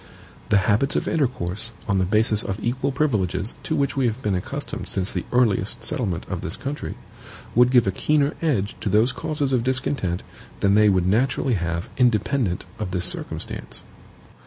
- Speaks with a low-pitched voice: Yes, low, 110 Hz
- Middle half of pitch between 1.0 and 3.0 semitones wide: No, wide, 5.4 semitones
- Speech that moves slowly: No, average, 175 wpm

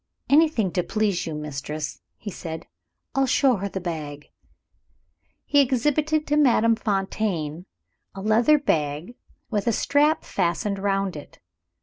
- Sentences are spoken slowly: Yes, slow, 130 wpm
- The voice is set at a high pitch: Yes, high, 200 Hz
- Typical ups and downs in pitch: No, wide, 7.8 semitones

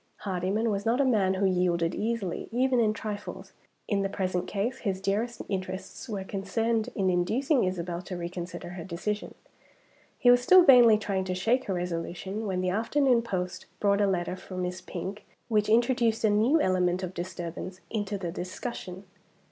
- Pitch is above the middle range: Yes, high, 195 Hz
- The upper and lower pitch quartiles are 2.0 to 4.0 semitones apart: Yes, average, 3.7 semitones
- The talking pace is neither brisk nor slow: Yes, average, 170 wpm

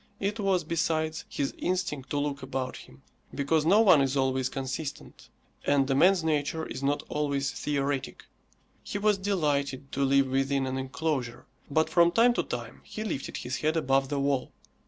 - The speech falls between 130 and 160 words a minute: No, average, 175 wpm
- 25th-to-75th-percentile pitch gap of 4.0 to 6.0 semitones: No, average, 3.3 semitones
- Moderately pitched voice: Yes, medium, 145 Hz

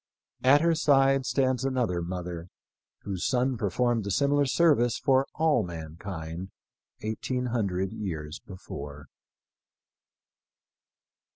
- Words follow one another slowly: Yes, slow, 105 wpm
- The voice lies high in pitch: No, low, 115 Hz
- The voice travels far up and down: Yes, wide, 6.9 semitones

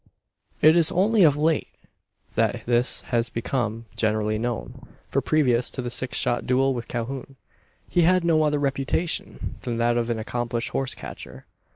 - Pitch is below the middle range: Yes, low, 125 Hz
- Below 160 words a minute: No, average, 165 wpm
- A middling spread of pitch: Yes, average, 4.2 semitones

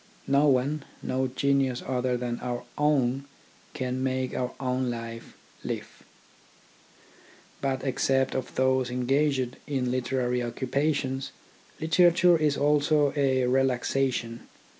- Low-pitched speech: Yes, low, 130 Hz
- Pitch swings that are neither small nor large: No, narrow, 1.9 semitones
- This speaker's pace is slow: Yes, slow, 115 wpm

